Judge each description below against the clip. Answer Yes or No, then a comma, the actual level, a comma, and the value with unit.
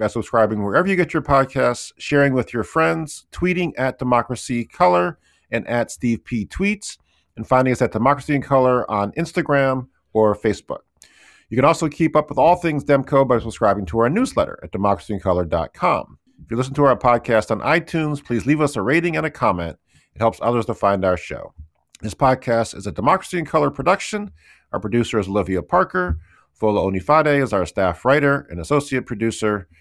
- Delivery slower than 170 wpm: No, average, 185 wpm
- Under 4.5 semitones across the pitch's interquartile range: No, wide, 5.5 semitones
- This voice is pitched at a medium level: No, low, 125 Hz